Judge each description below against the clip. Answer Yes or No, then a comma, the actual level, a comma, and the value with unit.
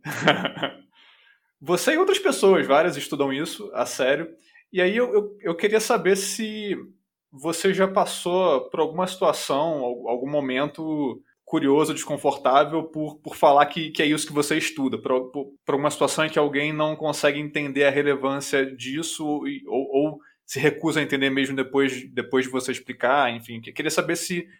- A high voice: No, medium, 150 Hz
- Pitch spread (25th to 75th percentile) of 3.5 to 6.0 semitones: Yes, average, 4.1 semitones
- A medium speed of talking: Yes, average, 165 wpm